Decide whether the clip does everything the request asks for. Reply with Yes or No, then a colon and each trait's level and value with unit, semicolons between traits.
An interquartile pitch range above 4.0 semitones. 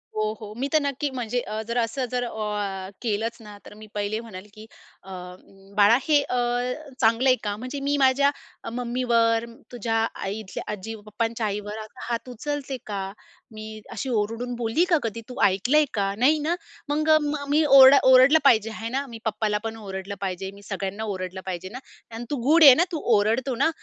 No: average, 3.7 semitones